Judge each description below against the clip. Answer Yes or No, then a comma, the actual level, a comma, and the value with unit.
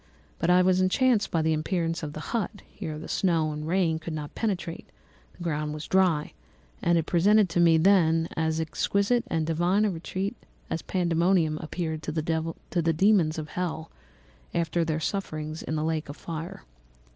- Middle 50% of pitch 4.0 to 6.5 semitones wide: No, average, 2.8 semitones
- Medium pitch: Yes, medium, 165 Hz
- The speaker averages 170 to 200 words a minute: Yes, average, 175 wpm